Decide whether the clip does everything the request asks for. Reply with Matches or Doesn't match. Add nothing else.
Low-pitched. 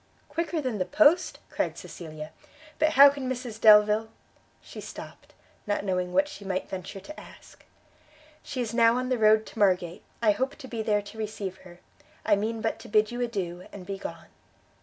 Doesn't match